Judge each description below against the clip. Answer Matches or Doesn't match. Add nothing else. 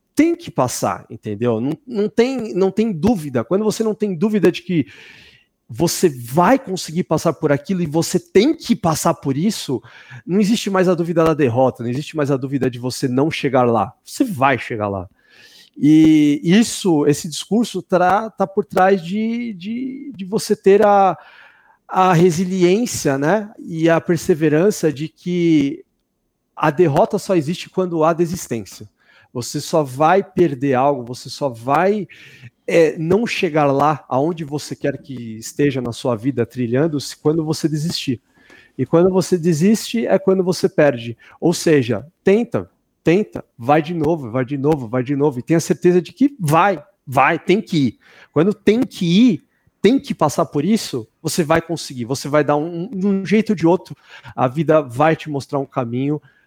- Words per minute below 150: Doesn't match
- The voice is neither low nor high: Matches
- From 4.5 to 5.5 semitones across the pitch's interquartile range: Matches